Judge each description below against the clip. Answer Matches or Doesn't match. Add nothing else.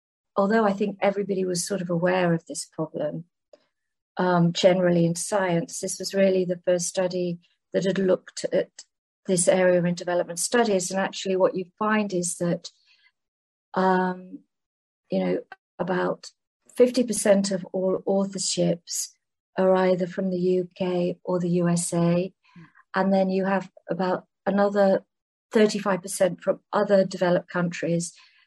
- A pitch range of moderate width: Doesn't match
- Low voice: Doesn't match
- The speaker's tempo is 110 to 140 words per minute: Matches